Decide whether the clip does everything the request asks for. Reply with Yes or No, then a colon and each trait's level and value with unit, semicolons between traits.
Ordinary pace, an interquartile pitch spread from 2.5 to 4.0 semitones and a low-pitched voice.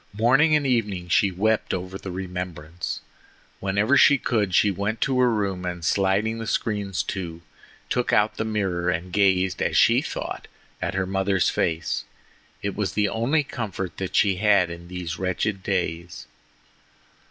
Yes: average, 160 wpm; average, 3.2 semitones; very low, 95 Hz